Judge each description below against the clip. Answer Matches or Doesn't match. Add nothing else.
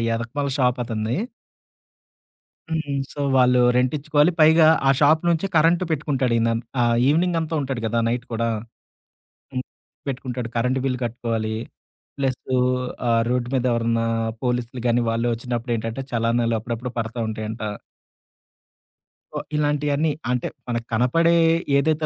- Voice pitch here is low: Matches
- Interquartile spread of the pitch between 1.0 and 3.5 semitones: Doesn't match